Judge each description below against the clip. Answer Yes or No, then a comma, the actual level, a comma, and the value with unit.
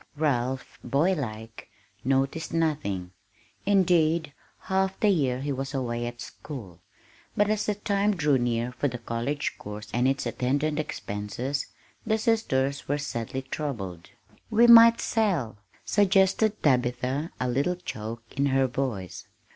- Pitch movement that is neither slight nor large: No, wide, 6.2 semitones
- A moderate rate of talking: No, slow, 130 wpm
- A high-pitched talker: No, low, 135 Hz